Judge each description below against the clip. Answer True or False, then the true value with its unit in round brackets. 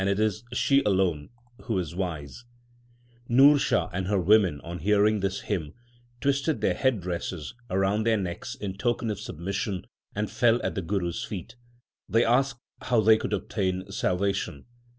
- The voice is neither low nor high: False (100 Hz)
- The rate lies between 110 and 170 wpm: True (150 wpm)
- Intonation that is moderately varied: True (4.2 semitones)